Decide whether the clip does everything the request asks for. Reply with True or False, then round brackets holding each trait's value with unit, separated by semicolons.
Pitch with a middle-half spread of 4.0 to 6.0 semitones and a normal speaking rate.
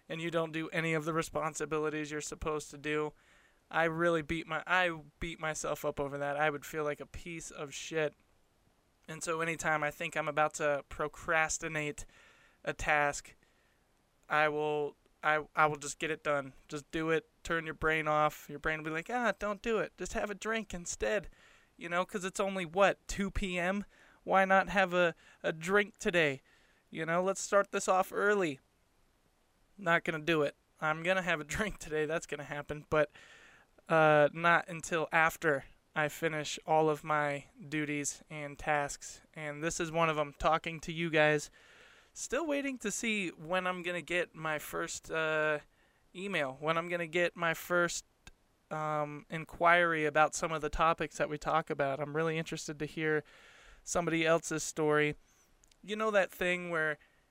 False (2.4 semitones; 185 wpm)